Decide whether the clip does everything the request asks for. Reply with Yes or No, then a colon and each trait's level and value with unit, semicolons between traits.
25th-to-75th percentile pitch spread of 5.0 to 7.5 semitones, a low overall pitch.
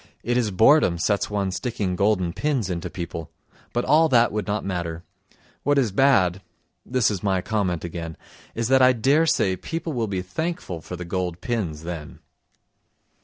Yes: wide, 5.6 semitones; low, 100 Hz